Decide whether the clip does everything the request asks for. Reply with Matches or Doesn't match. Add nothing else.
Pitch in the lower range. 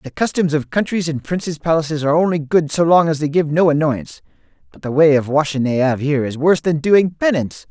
Doesn't match